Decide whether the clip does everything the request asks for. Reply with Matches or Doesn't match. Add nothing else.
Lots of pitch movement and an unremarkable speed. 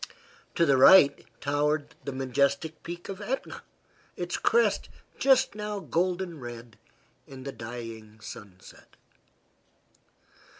Doesn't match